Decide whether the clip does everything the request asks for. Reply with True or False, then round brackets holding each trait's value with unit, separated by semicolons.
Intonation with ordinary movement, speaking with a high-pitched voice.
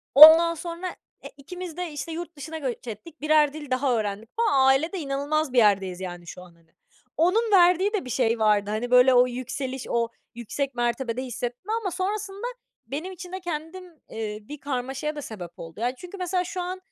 False (6.5 semitones; 280 Hz)